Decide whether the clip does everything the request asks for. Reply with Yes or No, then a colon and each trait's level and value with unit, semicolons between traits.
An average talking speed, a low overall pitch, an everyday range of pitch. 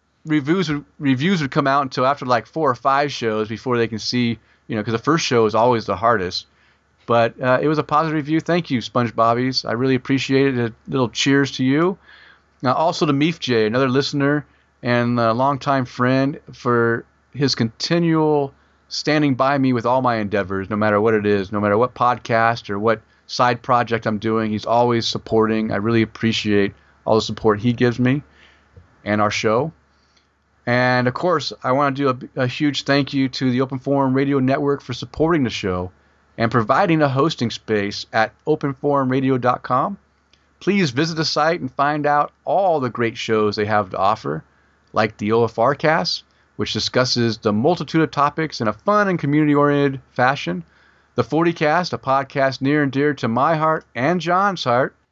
Yes: average, 185 wpm; low, 125 Hz; average, 4.4 semitones